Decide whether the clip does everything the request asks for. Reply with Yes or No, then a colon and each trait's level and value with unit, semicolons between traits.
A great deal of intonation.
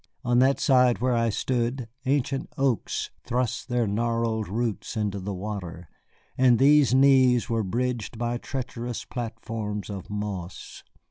No: average, 3.1 semitones